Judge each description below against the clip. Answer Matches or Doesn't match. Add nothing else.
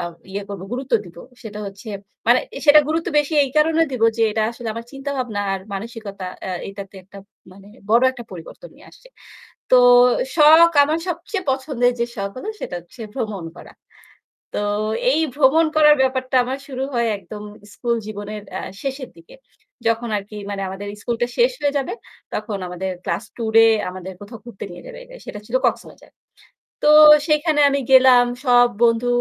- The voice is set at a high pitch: Matches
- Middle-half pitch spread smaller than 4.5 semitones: Doesn't match